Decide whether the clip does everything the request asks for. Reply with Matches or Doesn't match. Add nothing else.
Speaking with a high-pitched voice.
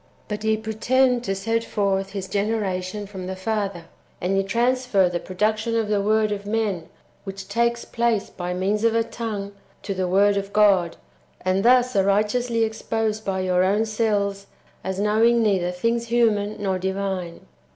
Matches